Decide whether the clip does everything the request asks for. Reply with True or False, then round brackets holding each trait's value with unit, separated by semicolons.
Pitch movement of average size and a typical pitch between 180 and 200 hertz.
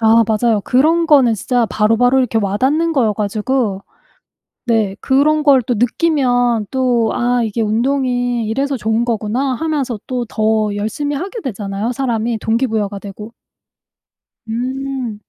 False (3.3 semitones; 240 Hz)